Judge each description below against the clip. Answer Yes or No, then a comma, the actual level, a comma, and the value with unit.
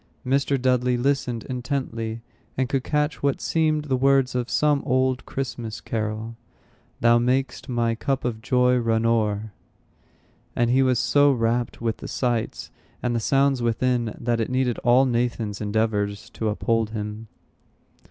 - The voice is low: Yes, low, 120 Hz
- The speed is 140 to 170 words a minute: Yes, average, 150 wpm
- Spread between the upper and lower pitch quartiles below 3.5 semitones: Yes, narrow, 2.6 semitones